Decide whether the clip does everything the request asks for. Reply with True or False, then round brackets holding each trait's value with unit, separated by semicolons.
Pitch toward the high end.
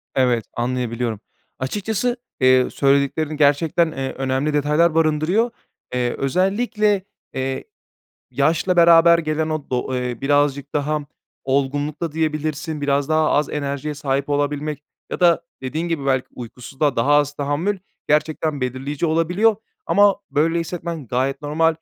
False (150 Hz)